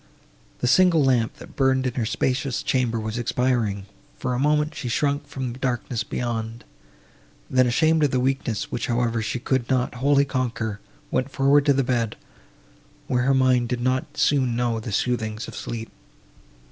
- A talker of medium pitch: No, low, 125 Hz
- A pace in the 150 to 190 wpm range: Yes, average, 175 wpm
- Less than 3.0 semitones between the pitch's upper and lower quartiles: Yes, narrow, 2.4 semitones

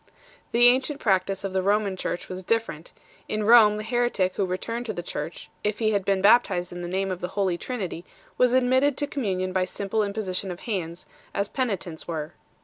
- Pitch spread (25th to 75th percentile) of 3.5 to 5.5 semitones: Yes, average, 3.8 semitones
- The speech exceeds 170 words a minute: Yes, fast, 205 wpm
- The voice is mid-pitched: No, high, 200 Hz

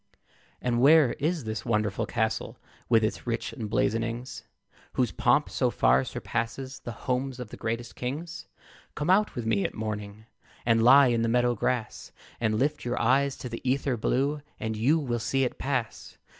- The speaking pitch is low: Yes, low, 120 Hz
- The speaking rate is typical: Yes, average, 170 wpm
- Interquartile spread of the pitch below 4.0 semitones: Yes, average, 3.2 semitones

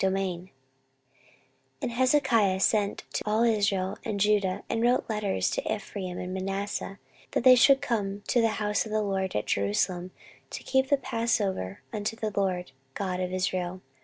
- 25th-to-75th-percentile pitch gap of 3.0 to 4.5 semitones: Yes, average, 3.4 semitones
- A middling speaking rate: Yes, average, 165 wpm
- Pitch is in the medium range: No, high, 205 Hz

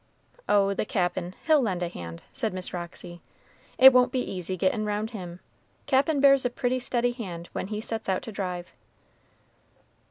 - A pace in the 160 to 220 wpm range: Yes, average, 170 wpm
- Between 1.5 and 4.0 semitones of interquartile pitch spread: No, wide, 5.5 semitones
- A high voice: Yes, high, 205 Hz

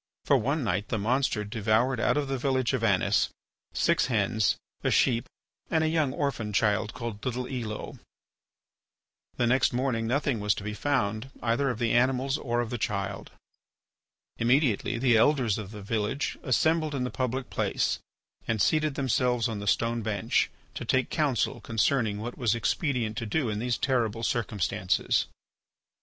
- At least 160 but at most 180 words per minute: Yes, average, 165 wpm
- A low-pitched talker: Yes, low, 120 Hz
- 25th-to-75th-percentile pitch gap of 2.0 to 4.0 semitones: Yes, average, 3.5 semitones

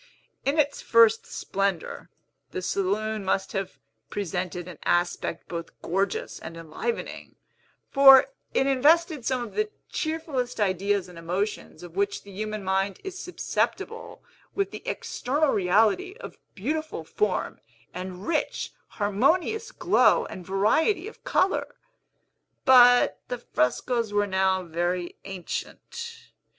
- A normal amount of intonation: No, wide, 7.3 semitones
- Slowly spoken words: Yes, slow, 120 wpm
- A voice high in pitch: Yes, high, 210 Hz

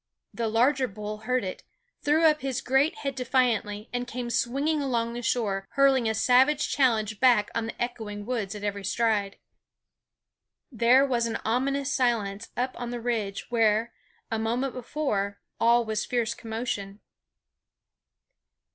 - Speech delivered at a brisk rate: No, average, 145 wpm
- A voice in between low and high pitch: No, high, 235 Hz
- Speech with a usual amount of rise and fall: Yes, average, 3.0 semitones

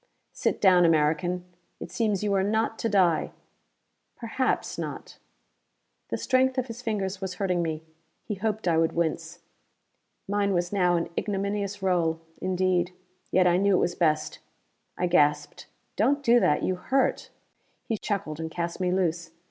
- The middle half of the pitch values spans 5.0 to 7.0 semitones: No, average, 3.2 semitones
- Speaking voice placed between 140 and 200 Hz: Yes, medium, 185 Hz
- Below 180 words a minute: Yes, average, 155 wpm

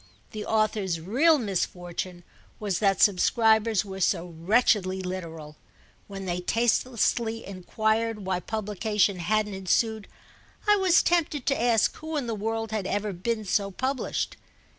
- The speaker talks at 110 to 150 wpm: Yes, slow, 135 wpm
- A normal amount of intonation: Yes, average, 3.3 semitones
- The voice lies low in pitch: No, high, 210 Hz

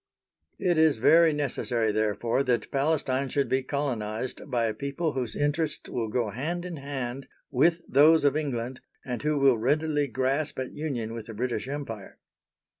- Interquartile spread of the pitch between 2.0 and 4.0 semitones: Yes, average, 3.7 semitones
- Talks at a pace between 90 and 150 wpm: No, average, 165 wpm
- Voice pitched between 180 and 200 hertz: No, low, 135 Hz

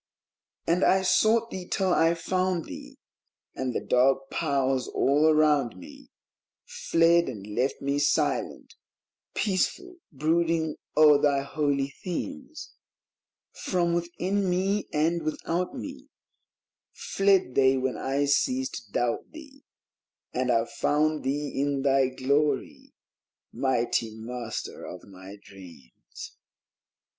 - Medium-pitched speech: Yes, medium, 150 Hz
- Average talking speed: No, slow, 115 wpm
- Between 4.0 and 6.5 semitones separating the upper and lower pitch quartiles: Yes, wide, 5.4 semitones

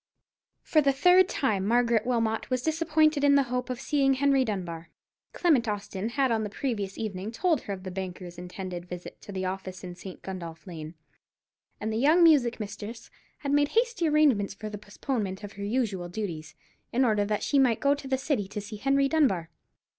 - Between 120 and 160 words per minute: No, average, 195 wpm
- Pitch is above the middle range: Yes, high, 220 Hz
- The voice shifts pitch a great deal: Yes, wide, 6.2 semitones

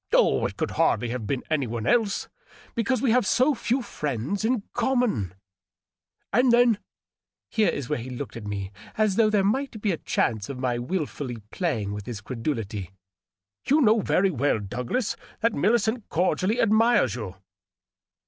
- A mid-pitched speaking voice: Yes, medium, 170 Hz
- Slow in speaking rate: No, average, 165 wpm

